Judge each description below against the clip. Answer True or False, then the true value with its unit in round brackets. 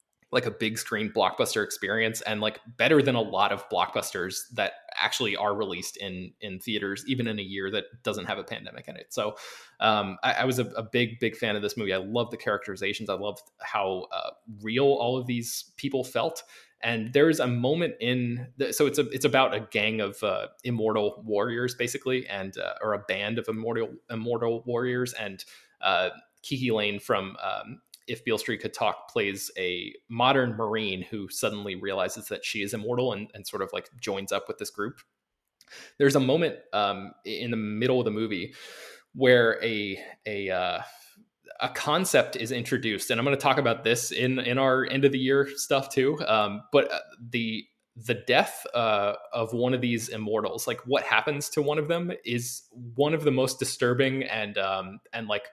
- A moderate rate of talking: True (195 wpm)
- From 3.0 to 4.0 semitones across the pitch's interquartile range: True (3.4 semitones)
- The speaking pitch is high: False (120 Hz)